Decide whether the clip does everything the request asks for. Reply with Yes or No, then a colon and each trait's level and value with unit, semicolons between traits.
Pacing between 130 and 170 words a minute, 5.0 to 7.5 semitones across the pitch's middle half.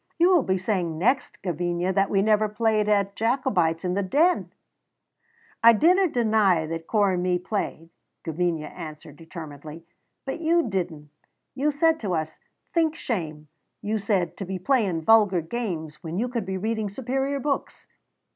Yes: average, 160 wpm; wide, 5.6 semitones